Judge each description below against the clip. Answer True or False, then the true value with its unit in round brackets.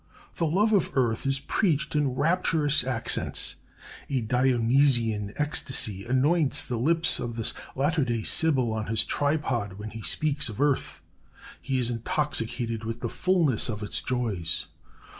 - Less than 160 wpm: True (145 wpm)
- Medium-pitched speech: False (130 Hz)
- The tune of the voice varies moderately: True (4.7 semitones)